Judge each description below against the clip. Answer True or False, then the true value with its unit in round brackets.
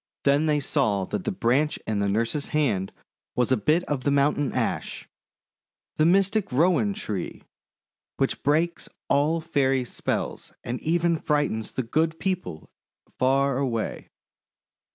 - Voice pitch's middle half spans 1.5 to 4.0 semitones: False (4.7 semitones)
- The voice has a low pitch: False (145 Hz)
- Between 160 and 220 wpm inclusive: False (145 wpm)